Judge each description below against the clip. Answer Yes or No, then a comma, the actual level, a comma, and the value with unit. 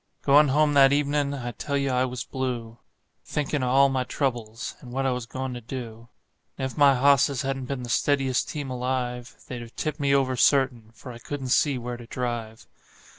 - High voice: No, low, 130 Hz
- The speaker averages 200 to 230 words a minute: Yes, fast, 205 wpm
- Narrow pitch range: Yes, narrow, 2.2 semitones